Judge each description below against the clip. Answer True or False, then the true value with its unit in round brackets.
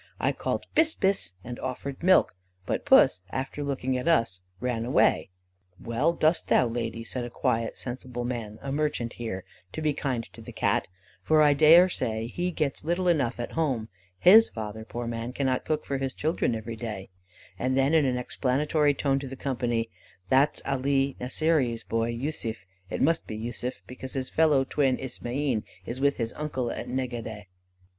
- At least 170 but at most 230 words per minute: True (175 wpm)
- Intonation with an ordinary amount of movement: True (4.0 semitones)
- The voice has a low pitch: True (130 Hz)